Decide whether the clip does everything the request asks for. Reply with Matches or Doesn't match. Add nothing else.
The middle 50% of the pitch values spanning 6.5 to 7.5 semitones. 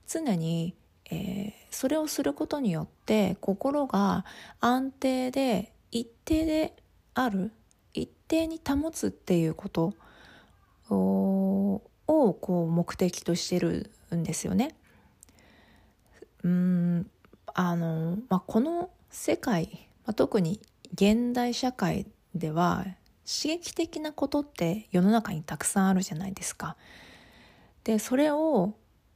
Matches